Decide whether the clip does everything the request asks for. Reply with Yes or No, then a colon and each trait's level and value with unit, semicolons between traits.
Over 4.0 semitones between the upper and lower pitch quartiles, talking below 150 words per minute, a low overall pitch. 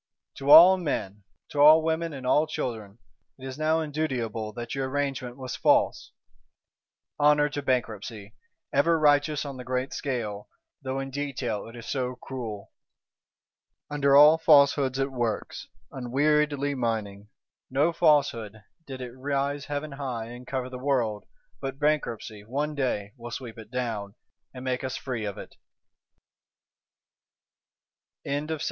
No: average, 3.5 semitones; average, 140 wpm; low, 130 Hz